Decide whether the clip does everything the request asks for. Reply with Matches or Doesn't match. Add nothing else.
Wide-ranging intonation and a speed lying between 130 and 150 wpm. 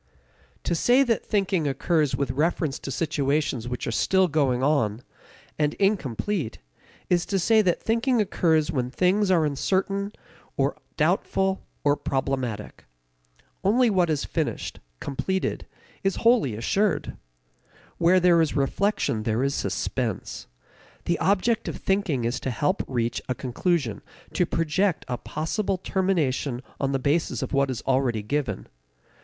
Matches